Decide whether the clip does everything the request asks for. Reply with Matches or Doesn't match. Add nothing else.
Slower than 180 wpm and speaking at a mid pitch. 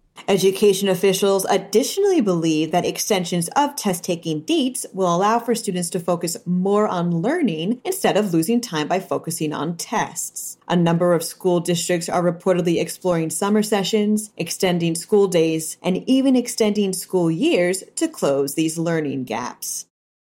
Matches